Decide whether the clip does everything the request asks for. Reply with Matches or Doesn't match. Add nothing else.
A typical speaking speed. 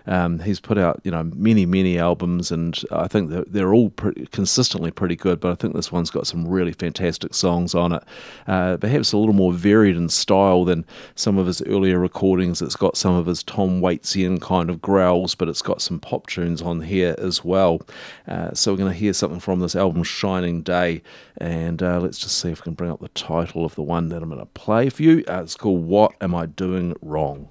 Doesn't match